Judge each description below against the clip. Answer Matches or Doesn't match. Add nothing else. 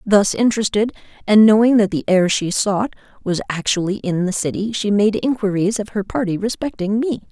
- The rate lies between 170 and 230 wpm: Matches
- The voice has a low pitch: Doesn't match